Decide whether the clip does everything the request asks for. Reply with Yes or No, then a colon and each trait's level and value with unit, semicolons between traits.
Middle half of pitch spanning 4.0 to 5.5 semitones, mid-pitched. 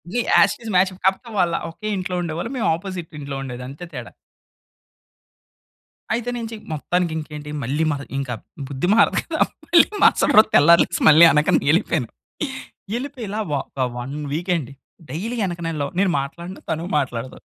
Yes: average, 5.2 semitones; medium, 170 Hz